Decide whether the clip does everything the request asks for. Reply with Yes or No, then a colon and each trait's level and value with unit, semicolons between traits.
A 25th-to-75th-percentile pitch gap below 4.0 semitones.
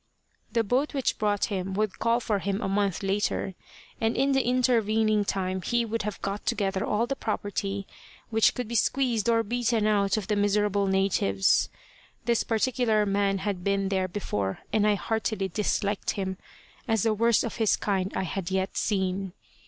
Yes: narrow, 2.5 semitones